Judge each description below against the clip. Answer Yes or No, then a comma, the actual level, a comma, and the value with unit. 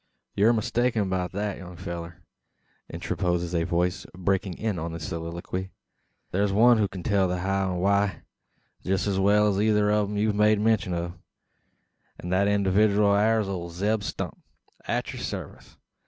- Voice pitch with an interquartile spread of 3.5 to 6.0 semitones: No, average, 2.8 semitones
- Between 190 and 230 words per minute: No, average, 170 wpm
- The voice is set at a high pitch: No, very low, 95 Hz